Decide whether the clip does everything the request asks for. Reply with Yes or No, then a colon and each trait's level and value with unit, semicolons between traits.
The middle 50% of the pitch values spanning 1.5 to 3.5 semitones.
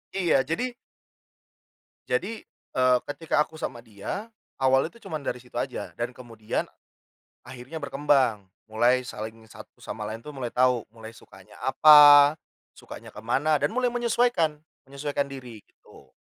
No: average, 4.3 semitones